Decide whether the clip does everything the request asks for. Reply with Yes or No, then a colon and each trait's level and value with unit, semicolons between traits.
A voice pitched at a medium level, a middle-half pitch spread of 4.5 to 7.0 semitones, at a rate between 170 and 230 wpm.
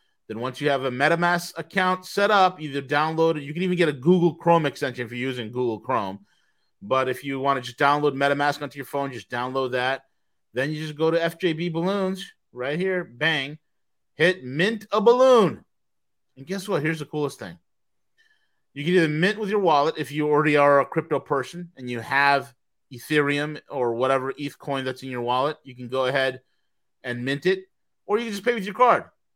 Yes: medium, 145 Hz; average, 4.8 semitones; fast, 205 wpm